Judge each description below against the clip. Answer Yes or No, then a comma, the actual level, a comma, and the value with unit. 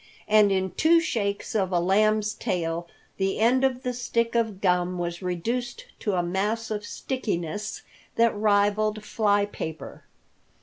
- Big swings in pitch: No, average, 3.5 semitones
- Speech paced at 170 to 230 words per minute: No, average, 145 wpm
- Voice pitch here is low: No, high, 210 Hz